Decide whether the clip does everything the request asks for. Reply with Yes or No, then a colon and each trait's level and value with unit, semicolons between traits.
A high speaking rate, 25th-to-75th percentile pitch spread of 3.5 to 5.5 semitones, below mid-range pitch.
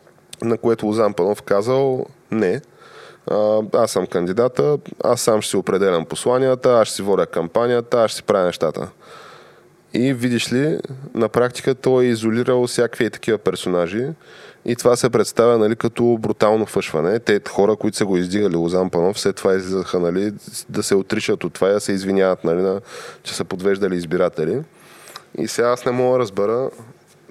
Yes: fast, 170 wpm; average, 4.0 semitones; low, 115 Hz